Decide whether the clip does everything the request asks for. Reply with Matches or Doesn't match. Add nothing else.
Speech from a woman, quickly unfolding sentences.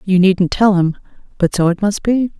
Matches